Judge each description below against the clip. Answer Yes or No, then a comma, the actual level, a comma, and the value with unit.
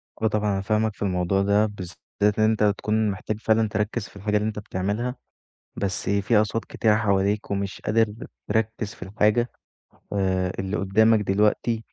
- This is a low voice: Yes, low, 105 Hz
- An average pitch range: No, narrow, 1.8 semitones